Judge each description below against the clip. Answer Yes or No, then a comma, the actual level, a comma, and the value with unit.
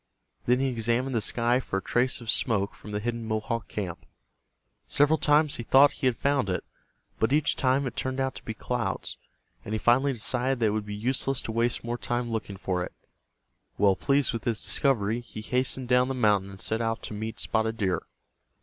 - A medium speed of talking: No, fast, 210 wpm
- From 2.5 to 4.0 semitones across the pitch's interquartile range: Yes, average, 3.4 semitones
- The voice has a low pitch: Yes, low, 115 Hz